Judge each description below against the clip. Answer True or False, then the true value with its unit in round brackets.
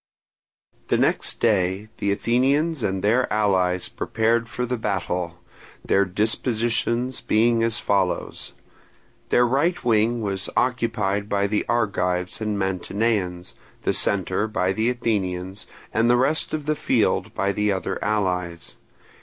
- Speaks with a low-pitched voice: True (105 Hz)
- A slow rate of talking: True (130 wpm)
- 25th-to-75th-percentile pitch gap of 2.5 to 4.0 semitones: True (3.7 semitones)